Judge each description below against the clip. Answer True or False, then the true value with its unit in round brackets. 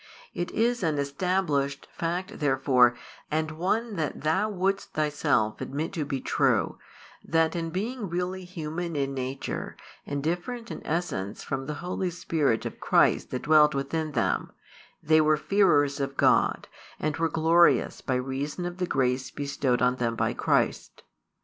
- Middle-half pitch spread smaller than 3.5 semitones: False (4.3 semitones)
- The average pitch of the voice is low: False (155 Hz)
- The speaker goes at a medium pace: True (150 wpm)